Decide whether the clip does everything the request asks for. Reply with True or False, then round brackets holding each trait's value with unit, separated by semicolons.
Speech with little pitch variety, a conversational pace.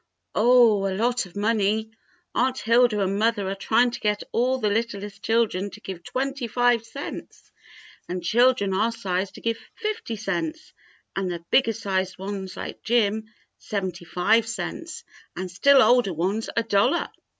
False (3.6 semitones; 160 wpm)